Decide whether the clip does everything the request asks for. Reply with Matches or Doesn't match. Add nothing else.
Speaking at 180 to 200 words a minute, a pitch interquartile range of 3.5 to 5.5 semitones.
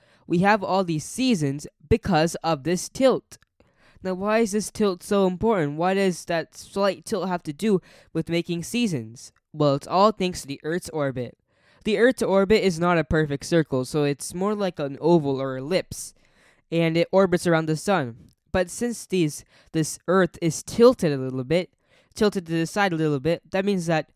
Matches